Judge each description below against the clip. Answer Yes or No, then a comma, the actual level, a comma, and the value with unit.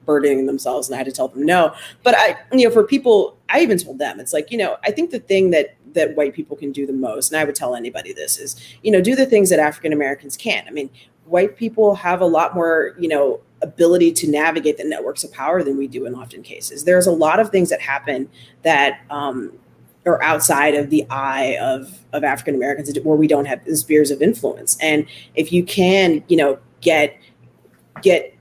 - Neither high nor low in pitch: Yes, medium, 155 Hz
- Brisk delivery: Yes, fast, 225 wpm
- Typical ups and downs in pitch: Yes, average, 4.2 semitones